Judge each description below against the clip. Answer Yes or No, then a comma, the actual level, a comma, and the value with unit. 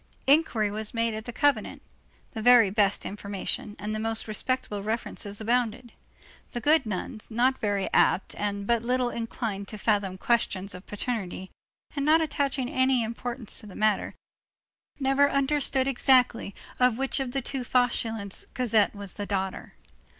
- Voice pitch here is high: Yes, high, 230 Hz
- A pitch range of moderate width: Yes, average, 3.7 semitones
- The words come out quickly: No, average, 155 wpm